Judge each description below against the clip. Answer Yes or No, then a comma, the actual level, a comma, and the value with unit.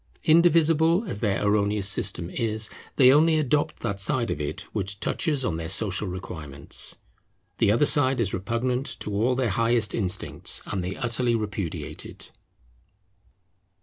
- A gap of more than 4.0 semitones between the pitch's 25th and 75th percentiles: Yes, average, 5.2 semitones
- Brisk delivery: No, average, 150 wpm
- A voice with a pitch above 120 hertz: No, low, 110 Hz